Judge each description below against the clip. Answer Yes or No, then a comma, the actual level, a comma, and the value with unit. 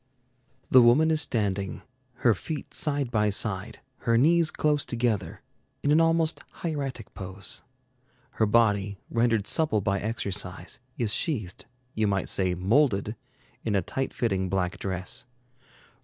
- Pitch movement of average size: No, wide, 5.9 semitones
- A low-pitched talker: Yes, low, 110 Hz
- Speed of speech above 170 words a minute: No, slow, 135 wpm